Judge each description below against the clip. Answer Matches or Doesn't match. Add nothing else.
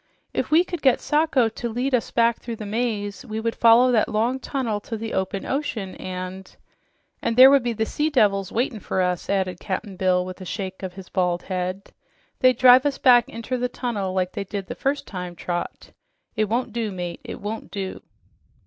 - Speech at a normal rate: Doesn't match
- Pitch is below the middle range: Doesn't match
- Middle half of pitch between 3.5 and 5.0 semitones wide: Matches